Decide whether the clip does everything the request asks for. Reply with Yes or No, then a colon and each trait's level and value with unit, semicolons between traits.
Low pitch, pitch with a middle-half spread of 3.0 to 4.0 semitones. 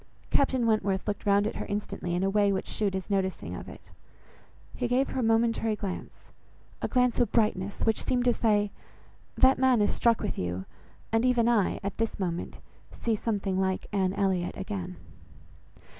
No: high, 210 Hz; average, 3.3 semitones